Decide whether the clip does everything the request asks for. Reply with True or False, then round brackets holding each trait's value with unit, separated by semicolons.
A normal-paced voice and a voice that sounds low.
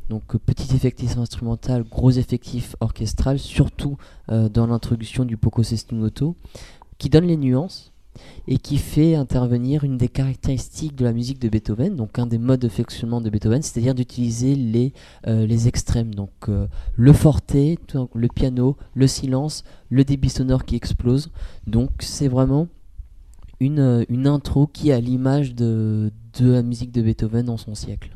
True (165 wpm; 120 Hz)